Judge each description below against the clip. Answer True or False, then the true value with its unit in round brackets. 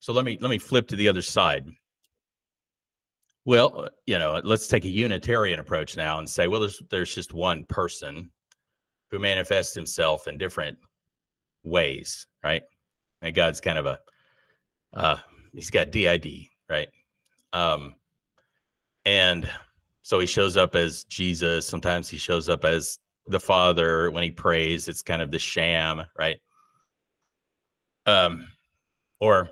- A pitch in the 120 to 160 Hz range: False (90 Hz)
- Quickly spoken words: False (140 wpm)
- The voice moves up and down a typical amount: True (4.1 semitones)